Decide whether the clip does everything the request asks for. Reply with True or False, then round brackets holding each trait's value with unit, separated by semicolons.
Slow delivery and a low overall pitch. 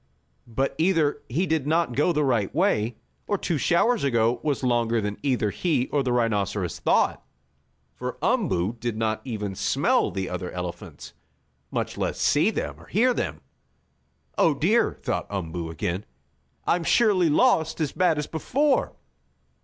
False (155 wpm; 130 Hz)